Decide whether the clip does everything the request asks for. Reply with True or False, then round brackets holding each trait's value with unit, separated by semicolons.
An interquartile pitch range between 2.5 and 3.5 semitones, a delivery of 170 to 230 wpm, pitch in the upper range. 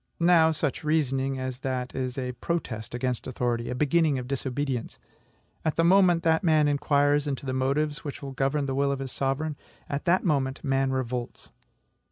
False (2.8 semitones; 175 wpm; 135 Hz)